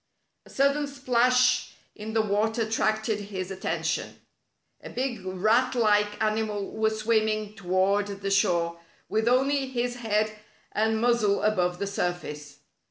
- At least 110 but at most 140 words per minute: Yes, slow, 135 wpm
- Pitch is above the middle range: Yes, high, 215 Hz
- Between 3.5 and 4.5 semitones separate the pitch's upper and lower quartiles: No, average, 3.0 semitones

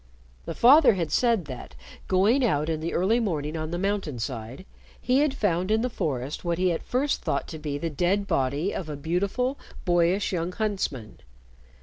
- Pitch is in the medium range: Yes, medium, 175 Hz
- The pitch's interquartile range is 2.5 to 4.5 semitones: No, wide, 5.4 semitones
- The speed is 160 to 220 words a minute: Yes, average, 190 wpm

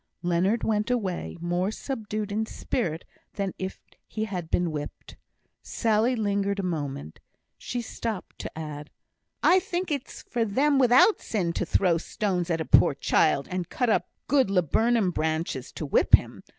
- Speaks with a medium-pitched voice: No, high, 200 Hz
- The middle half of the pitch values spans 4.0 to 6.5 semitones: Yes, average, 5.2 semitones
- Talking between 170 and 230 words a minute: No, average, 160 wpm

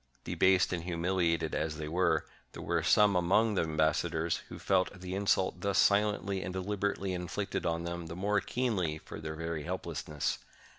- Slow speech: No, average, 165 wpm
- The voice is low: Yes, very low, 90 Hz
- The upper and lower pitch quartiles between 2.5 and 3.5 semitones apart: Yes, average, 3.0 semitones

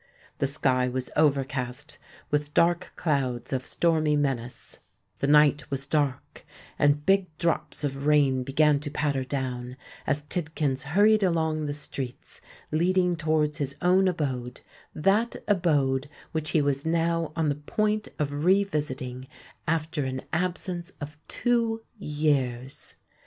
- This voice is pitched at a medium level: Yes, medium, 150 Hz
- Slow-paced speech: Yes, slow, 130 wpm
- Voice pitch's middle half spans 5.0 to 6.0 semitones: No, average, 3.7 semitones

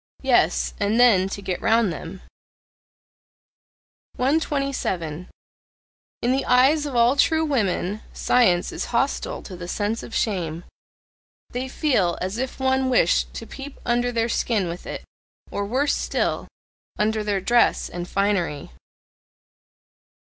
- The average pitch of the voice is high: Yes, high, 225 Hz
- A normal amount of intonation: No, wide, 5.8 semitones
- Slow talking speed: Yes, slow, 130 wpm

